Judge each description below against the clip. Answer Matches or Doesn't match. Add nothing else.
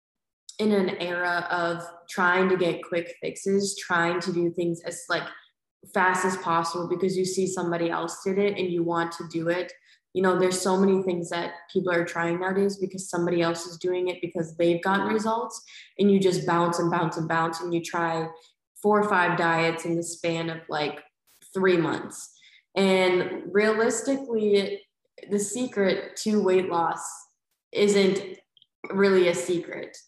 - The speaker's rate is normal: Matches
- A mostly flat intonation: Matches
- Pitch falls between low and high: Matches